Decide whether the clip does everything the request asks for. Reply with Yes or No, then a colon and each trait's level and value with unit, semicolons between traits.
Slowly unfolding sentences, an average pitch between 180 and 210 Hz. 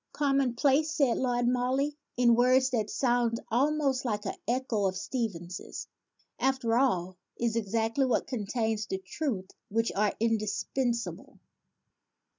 No: slow, 125 wpm; high, 240 Hz